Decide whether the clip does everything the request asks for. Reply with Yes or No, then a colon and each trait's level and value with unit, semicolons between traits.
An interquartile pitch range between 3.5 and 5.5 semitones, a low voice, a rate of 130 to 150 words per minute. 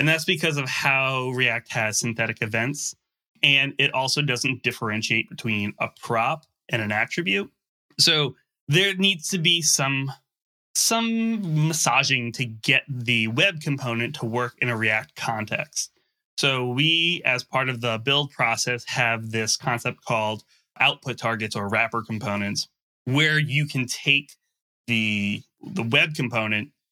Yes: average, 4.5 semitones; low, 130 Hz; average, 145 wpm